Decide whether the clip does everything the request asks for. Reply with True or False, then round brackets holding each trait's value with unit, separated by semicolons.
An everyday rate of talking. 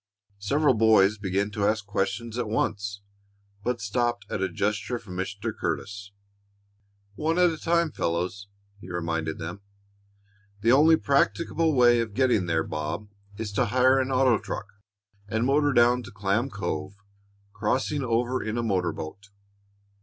True (150 wpm)